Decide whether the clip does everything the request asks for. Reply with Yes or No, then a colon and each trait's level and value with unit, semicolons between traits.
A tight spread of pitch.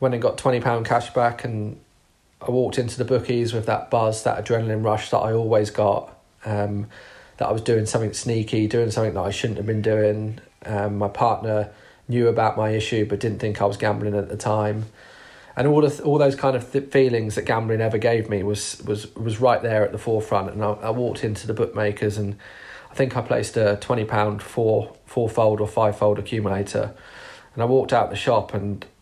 Yes: narrow, 2.1 semitones